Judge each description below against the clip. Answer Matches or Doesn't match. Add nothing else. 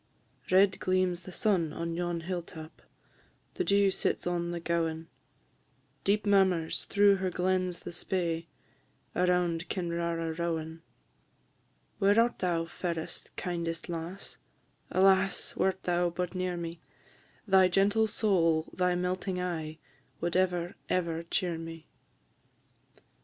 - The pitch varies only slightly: Matches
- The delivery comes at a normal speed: Doesn't match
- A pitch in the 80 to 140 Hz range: Doesn't match